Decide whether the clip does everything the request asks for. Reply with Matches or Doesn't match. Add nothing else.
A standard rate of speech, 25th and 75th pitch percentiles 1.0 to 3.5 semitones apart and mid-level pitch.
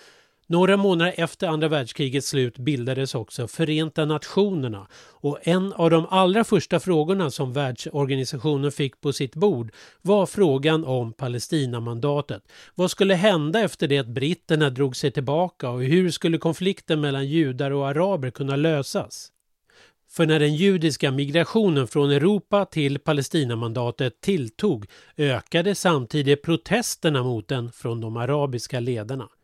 Doesn't match